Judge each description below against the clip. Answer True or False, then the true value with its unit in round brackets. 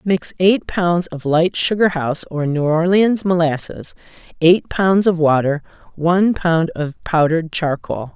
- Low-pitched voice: False (170 Hz)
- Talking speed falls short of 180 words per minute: True (145 wpm)